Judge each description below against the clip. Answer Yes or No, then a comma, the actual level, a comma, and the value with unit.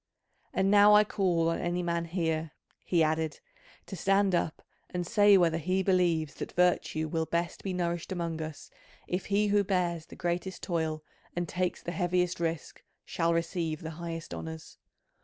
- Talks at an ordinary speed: Yes, average, 170 wpm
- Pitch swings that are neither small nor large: No, narrow, 2.1 semitones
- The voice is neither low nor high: Yes, medium, 175 Hz